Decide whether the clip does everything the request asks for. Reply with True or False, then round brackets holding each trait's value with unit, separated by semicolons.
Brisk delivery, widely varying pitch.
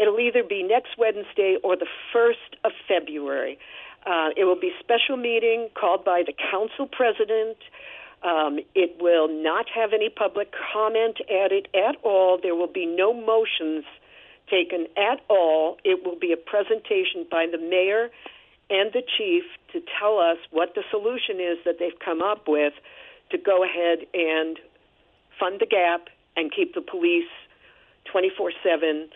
False (155 wpm; 6.6 semitones)